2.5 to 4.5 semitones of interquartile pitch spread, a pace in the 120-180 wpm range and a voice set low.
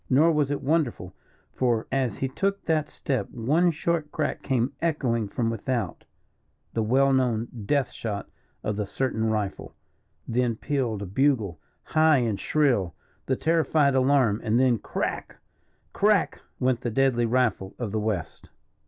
Yes: average, 4.2 semitones; average, 150 wpm; low, 125 Hz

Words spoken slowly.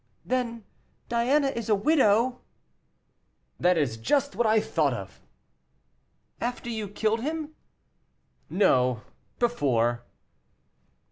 Yes: slow, 95 wpm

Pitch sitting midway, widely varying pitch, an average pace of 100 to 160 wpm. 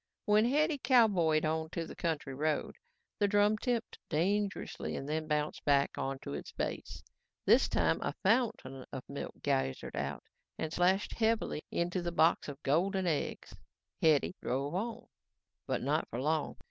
Yes: medium, 170 Hz; wide, 5.8 semitones; average, 150 wpm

